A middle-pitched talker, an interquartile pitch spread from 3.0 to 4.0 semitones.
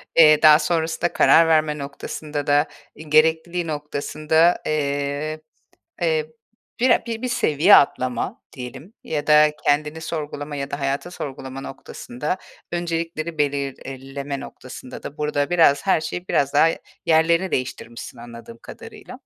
No: medium, 150 Hz; narrow, 2.6 semitones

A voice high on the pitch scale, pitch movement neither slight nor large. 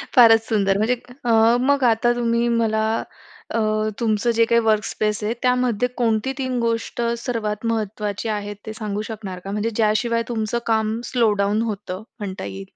No: high, 220 Hz; narrow, 1.8 semitones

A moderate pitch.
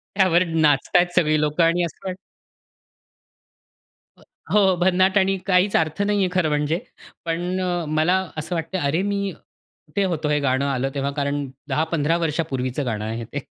Yes: medium, 165 Hz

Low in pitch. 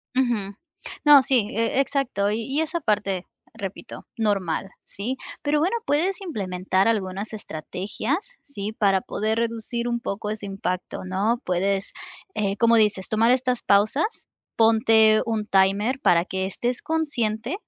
No: high, 220 Hz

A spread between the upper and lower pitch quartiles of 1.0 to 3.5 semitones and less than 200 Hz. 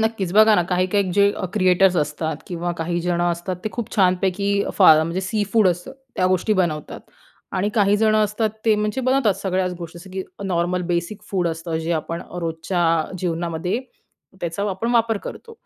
Yes: average, 3.2 semitones; medium, 185 Hz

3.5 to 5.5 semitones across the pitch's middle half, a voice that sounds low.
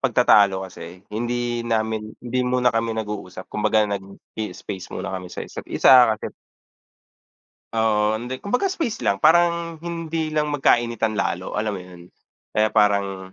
Yes: average, 4.0 semitones; low, 110 Hz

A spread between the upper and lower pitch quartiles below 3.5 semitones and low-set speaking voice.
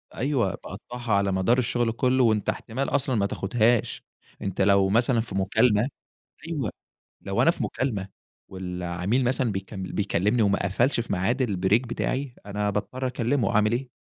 No: average, 4.1 semitones; low, 110 Hz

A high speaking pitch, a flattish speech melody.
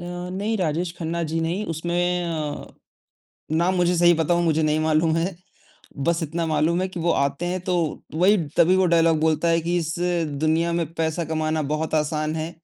No: medium, 165 Hz; narrow, 1.7 semitones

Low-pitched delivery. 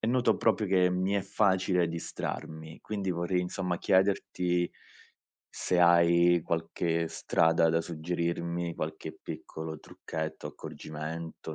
Yes: very low, 85 Hz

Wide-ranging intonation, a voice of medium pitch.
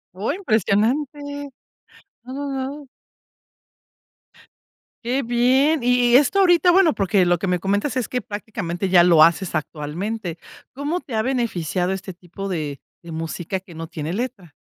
No: wide, 7.2 semitones; high, 215 Hz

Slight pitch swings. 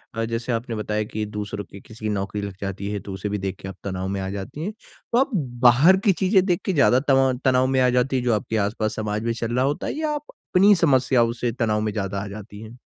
No: average, 4.2 semitones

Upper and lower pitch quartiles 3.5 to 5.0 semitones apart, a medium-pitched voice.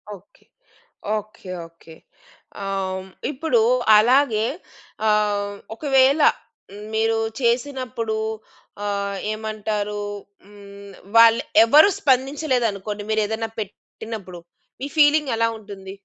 No: average, 4.0 semitones; high, 220 Hz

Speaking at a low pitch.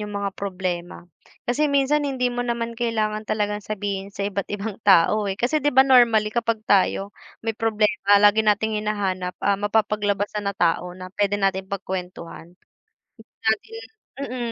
No: high, 210 Hz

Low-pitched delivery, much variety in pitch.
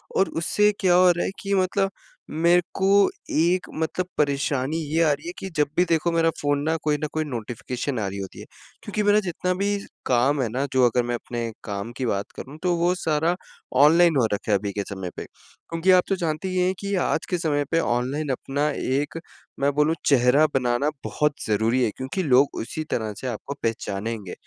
No: medium, 145 Hz; wide, 6.0 semitones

